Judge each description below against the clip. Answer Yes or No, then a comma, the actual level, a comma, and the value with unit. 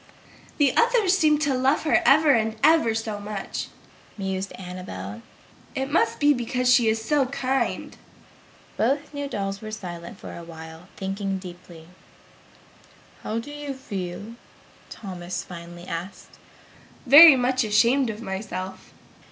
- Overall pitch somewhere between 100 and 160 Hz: No, high, 220 Hz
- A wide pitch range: Yes, wide, 6.6 semitones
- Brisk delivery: No, slow, 135 wpm